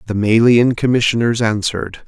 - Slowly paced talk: Yes, slow, 115 wpm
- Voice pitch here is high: No, low, 115 Hz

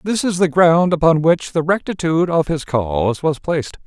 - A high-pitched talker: No, medium, 160 Hz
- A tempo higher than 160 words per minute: Yes, average, 200 wpm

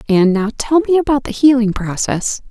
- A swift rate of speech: No, average, 190 wpm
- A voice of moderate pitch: No, high, 235 Hz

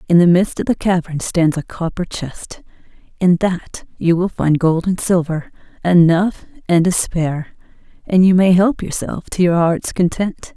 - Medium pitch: Yes, medium, 175 Hz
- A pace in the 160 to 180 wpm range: Yes, average, 175 wpm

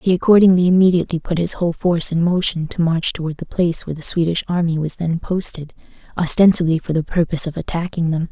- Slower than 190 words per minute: No, average, 200 wpm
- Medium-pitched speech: Yes, medium, 170 Hz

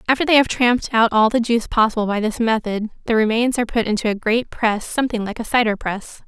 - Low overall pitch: No, high, 225 Hz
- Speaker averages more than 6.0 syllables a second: Yes, 6.3 syllables/s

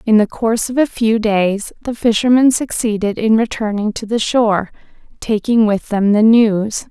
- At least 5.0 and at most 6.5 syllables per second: No, 4.7 syllables/s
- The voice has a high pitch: Yes, high, 220 Hz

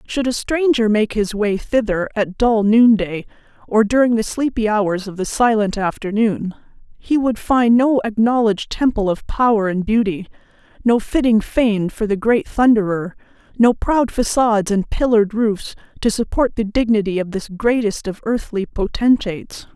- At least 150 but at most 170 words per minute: Yes, average, 160 wpm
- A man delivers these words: No, female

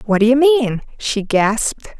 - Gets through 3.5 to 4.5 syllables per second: Yes, 4.4 syllables/s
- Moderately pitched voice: No, high, 240 Hz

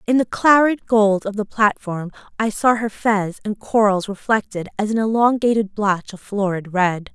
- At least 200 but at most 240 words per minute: No, average, 175 wpm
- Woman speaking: Yes, female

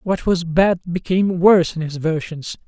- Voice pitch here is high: No, medium, 175 Hz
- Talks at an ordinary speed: Yes, average, 180 wpm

